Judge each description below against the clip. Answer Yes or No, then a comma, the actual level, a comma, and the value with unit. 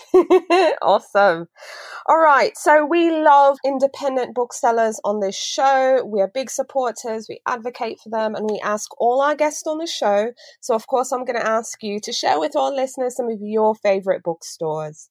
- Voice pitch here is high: Yes, high, 245 Hz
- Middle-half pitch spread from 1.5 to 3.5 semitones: No, average, 4.5 semitones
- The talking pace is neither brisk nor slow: Yes, average, 185 wpm